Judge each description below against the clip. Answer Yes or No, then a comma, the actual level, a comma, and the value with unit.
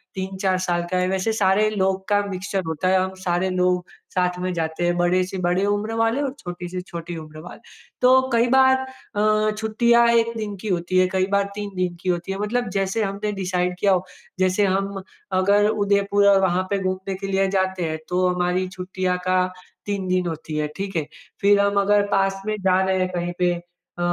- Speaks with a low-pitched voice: No, high, 190 Hz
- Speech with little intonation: Yes, narrow, 2.0 semitones